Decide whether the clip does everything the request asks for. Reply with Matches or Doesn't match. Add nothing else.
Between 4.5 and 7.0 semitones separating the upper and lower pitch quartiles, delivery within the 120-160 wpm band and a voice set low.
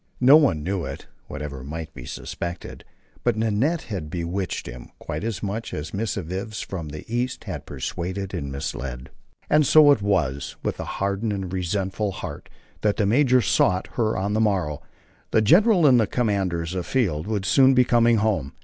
Doesn't match